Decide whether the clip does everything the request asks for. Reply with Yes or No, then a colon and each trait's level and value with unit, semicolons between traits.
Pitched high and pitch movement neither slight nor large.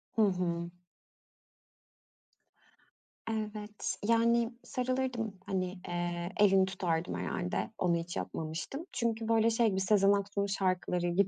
Yes: high, 195 Hz; average, 4.1 semitones